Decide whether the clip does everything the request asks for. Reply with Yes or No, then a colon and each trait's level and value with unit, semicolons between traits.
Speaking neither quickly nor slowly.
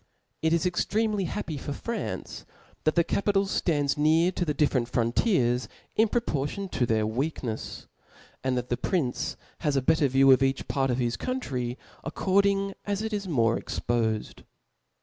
Yes: average, 165 wpm